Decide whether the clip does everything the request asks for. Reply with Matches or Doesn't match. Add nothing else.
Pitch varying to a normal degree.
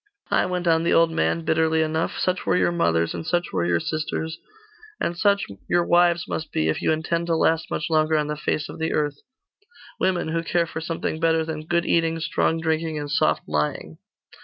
Doesn't match